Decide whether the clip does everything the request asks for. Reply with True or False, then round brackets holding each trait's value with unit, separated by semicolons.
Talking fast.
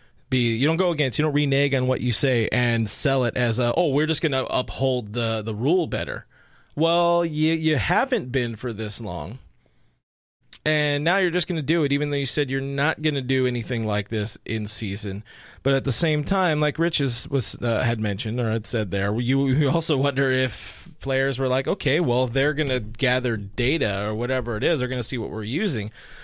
True (225 wpm)